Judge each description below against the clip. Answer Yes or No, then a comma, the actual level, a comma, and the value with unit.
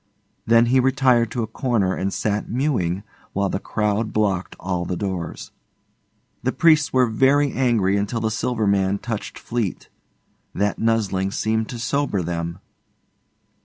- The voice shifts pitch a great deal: No, average, 3.7 semitones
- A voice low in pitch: Yes, low, 110 Hz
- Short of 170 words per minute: Yes, average, 145 wpm